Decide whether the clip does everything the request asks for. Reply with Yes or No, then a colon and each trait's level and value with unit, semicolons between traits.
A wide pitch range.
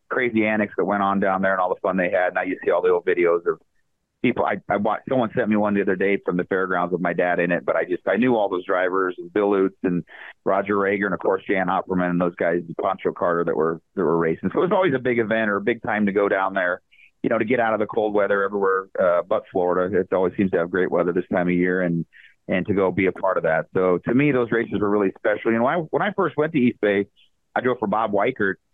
No: average, 4.4 semitones